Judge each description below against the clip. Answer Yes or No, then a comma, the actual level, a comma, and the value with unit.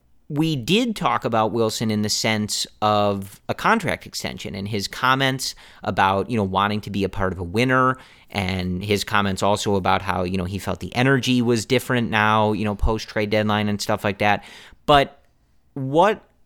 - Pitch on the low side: Yes, low, 105 Hz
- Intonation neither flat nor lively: Yes, average, 3.6 semitones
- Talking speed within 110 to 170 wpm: No, average, 190 wpm